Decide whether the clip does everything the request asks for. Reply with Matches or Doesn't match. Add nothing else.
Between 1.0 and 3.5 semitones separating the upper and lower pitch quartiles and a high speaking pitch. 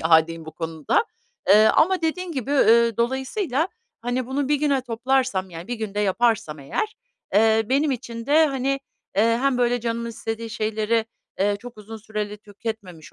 Doesn't match